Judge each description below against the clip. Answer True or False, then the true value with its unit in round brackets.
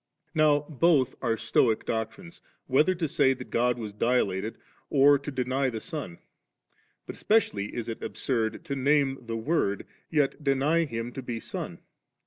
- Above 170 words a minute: False (155 wpm)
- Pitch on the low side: True (130 Hz)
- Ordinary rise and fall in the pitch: True (4.3 semitones)